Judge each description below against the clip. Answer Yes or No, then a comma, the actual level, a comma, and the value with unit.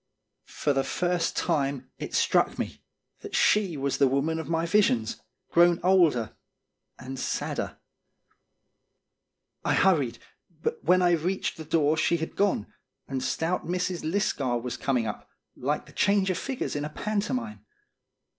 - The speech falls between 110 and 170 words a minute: Yes, average, 145 wpm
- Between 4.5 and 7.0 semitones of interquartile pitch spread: Yes, average, 5.0 semitones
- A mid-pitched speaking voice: Yes, medium, 160 Hz